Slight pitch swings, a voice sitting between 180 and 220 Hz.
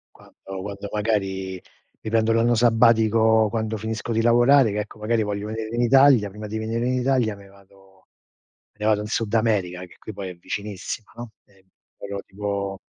No: narrow, 2.3 semitones; low, 110 Hz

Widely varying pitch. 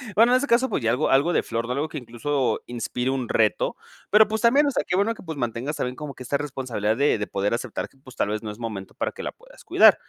Yes: wide, 7.0 semitones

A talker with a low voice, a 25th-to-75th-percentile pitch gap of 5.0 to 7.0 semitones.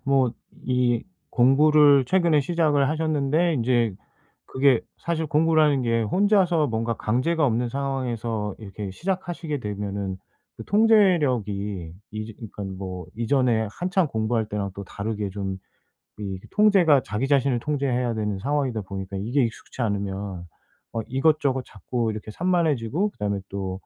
Yes: low, 125 Hz; wide, 6.3 semitones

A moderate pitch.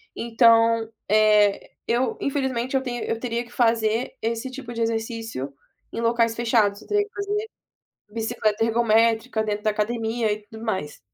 No: high, 230 Hz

